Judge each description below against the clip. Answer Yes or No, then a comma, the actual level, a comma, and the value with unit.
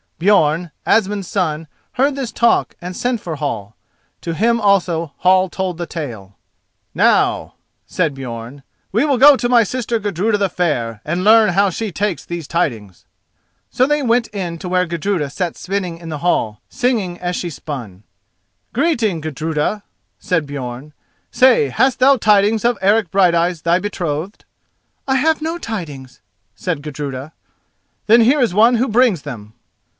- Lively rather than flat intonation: Yes, wide, 6.6 semitones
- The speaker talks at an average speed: Yes, average, 155 wpm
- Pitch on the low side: No, medium, 180 Hz